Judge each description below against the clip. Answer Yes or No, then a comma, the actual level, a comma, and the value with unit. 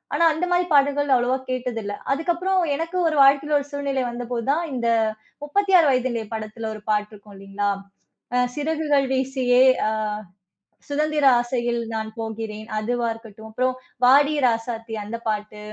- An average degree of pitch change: Yes, average, 4.5 semitones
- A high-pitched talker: Yes, very high, 250 Hz